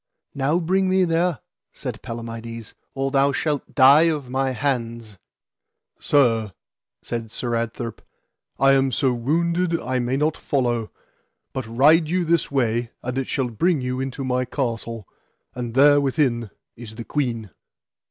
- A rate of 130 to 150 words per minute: Yes, average, 145 wpm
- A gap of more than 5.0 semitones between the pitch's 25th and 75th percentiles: No, average, 3.8 semitones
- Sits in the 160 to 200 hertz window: No, low, 130 Hz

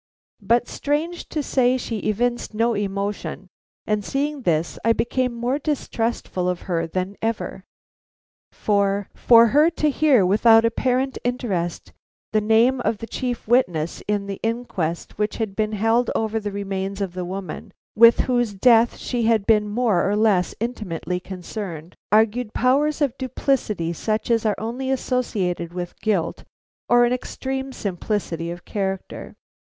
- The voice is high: Yes, high, 220 Hz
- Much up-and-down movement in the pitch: No, average, 4.0 semitones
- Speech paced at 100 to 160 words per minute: Yes, average, 150 wpm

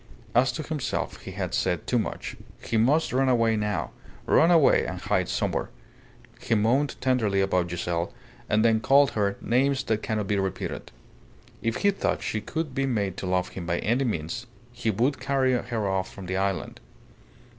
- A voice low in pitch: Yes, low, 110 Hz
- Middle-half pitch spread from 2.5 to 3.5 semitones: No, average, 5.2 semitones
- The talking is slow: No, average, 180 wpm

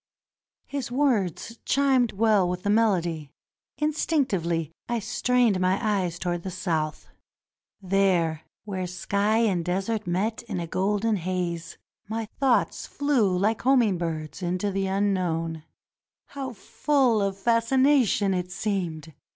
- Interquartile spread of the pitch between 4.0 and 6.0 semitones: Yes, average, 4.5 semitones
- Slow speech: Yes, slow, 125 wpm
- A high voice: Yes, high, 195 Hz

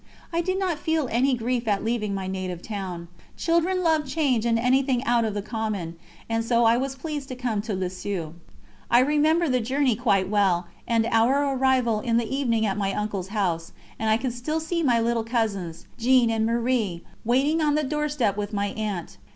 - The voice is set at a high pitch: Yes, high, 235 Hz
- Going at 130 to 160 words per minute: No, average, 195 wpm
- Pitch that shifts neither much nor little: Yes, average, 4.6 semitones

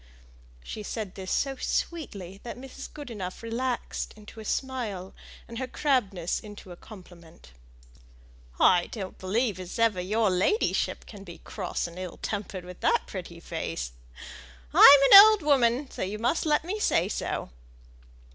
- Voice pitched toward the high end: Yes, high, 210 Hz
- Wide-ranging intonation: Yes, wide, 5.7 semitones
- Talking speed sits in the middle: Yes, average, 150 wpm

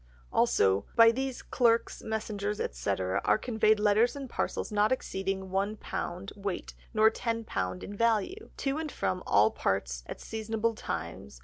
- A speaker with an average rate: Yes, average, 155 wpm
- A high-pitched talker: Yes, high, 215 Hz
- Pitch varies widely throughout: No, average, 3.5 semitones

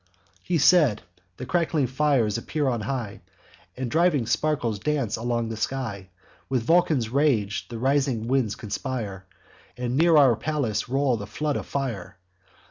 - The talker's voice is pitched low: Yes, low, 130 Hz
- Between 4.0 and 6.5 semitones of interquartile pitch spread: Yes, average, 4.5 semitones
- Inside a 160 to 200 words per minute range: No, average, 145 wpm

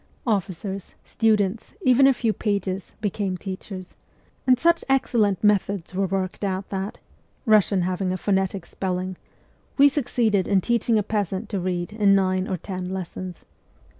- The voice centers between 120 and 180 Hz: No, high, 195 Hz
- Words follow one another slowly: No, average, 145 wpm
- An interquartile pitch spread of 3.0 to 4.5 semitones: No, narrow, 2.6 semitones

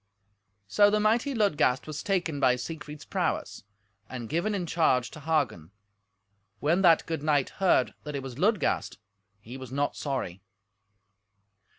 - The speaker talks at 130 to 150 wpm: Yes, average, 145 wpm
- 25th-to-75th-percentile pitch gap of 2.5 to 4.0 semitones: No, wide, 5.6 semitones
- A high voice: No, medium, 150 Hz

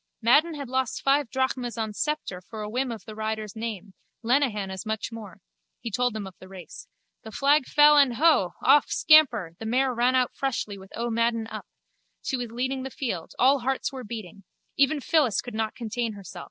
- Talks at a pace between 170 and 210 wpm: Yes, average, 200 wpm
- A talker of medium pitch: No, high, 235 Hz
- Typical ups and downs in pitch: Yes, average, 3.7 semitones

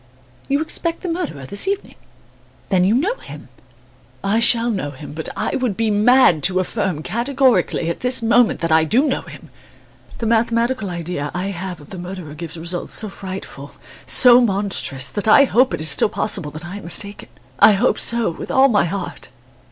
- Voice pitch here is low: No, high, 200 Hz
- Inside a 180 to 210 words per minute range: Yes, average, 190 wpm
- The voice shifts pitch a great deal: Yes, wide, 5.8 semitones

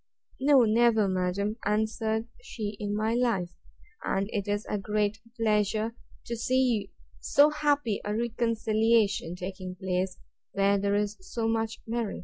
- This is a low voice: No, high, 215 Hz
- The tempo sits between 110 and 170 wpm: Yes, slow, 135 wpm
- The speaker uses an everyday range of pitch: No, narrow, 2.3 semitones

